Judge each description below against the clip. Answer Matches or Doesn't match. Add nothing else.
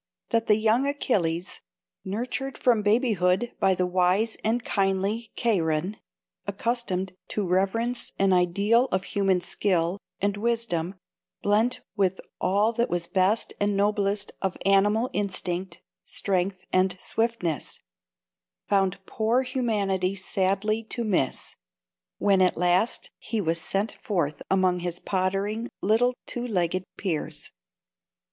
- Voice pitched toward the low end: Doesn't match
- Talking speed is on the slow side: Matches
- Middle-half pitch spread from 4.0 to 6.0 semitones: Doesn't match